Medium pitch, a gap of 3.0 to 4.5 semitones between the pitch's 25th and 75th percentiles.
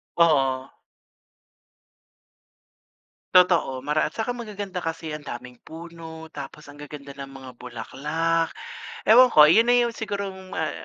No: medium, 160 Hz; average, 4.9 semitones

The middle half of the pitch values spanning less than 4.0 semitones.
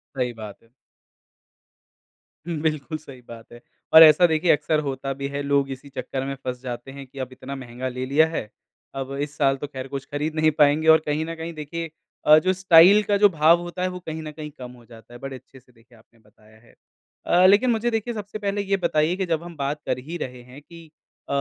No: average, 4.3 semitones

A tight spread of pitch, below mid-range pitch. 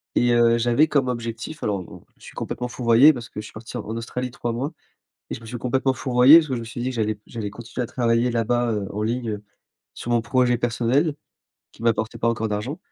Yes: narrow, 1.7 semitones; low, 120 Hz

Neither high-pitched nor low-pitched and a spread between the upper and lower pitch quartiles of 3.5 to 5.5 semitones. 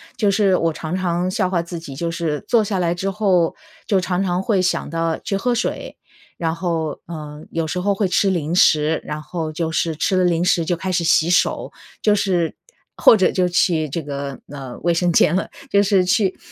No: medium, 175 Hz; narrow, 2.6 semitones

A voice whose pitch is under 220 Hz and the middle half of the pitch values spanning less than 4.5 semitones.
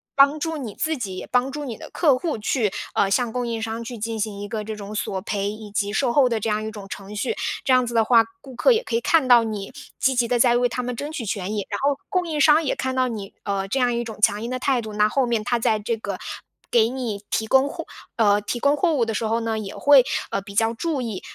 No: high, 230 Hz; average, 3.5 semitones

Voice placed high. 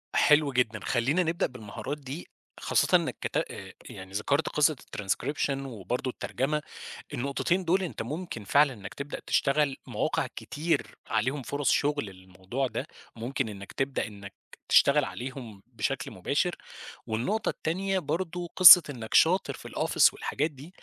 No: medium, 140 Hz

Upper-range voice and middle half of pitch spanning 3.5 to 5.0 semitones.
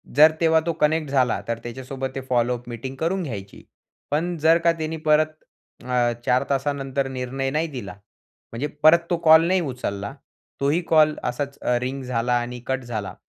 No: low, 135 Hz; average, 4.1 semitones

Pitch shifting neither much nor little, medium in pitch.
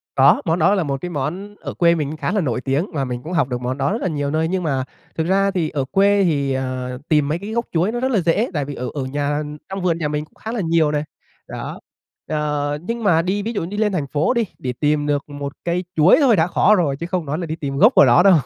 Yes: average, 4.8 semitones; medium, 160 Hz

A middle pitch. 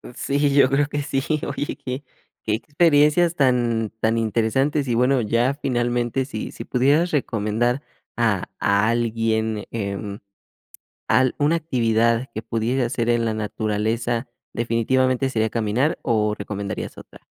No: low, 120 Hz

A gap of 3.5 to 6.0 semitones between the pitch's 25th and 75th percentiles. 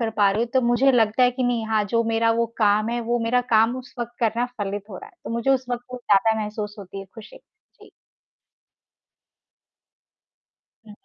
No: narrow, 2.4 semitones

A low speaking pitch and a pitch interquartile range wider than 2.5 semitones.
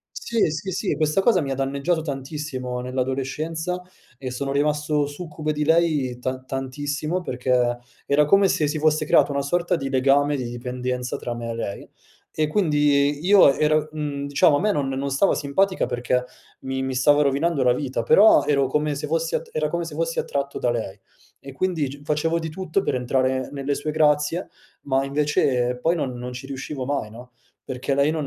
No: medium, 145 Hz; average, 2.9 semitones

